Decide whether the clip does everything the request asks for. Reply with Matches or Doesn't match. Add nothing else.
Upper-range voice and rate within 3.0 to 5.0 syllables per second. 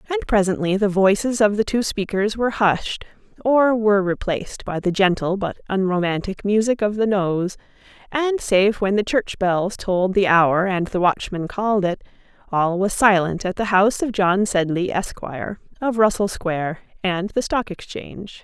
Matches